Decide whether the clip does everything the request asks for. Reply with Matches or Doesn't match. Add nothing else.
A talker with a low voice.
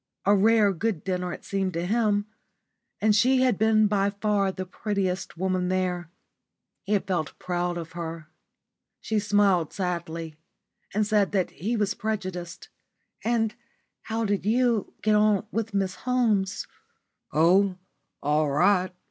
Doesn't match